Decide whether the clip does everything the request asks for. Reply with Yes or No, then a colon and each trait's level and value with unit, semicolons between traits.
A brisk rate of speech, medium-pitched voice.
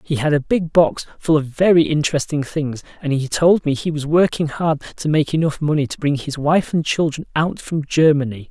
Yes: fast, 220 wpm; medium, 150 Hz